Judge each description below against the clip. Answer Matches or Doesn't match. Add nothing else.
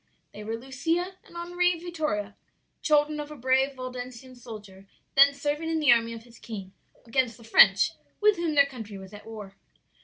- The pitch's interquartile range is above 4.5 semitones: Matches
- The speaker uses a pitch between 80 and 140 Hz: Doesn't match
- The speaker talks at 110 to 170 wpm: Doesn't match